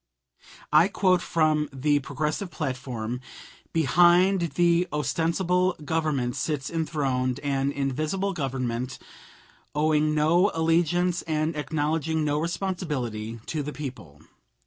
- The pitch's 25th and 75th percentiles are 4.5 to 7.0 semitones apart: No, average, 3.7 semitones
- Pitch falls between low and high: Yes, medium, 155 Hz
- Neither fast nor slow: No, slow, 100 wpm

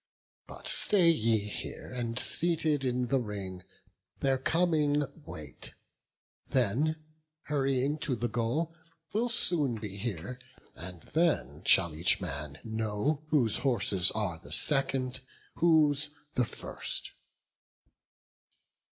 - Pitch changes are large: Yes, wide, 6.3 semitones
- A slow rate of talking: Yes, slow, 110 wpm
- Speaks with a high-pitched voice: No, low, 125 Hz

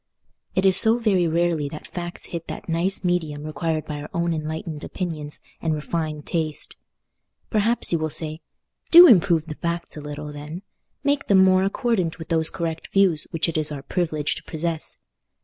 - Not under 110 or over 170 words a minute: No, average, 180 wpm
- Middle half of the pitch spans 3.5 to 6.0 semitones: No, average, 2.9 semitones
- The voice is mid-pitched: Yes, medium, 165 Hz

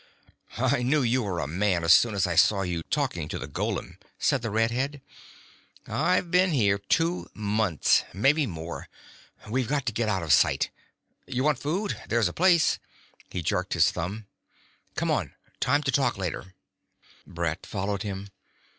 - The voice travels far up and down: Yes, wide, 6.9 semitones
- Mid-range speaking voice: No, low, 110 Hz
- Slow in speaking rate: No, average, 175 wpm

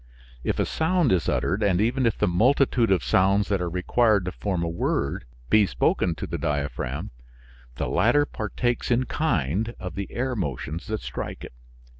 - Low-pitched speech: Yes, low, 100 Hz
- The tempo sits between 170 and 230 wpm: Yes, average, 180 wpm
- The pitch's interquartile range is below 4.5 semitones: No, average, 5.2 semitones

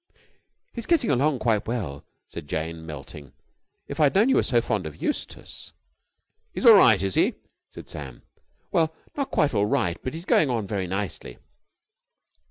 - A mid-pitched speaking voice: No, low, 110 Hz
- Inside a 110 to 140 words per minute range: No, average, 170 wpm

